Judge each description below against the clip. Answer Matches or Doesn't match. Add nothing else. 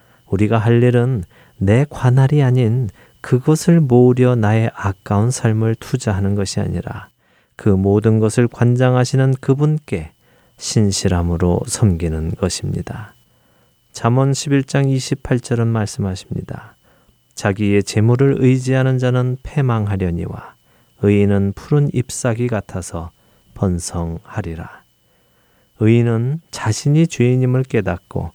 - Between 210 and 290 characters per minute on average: Matches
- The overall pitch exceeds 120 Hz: Doesn't match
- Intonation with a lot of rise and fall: Doesn't match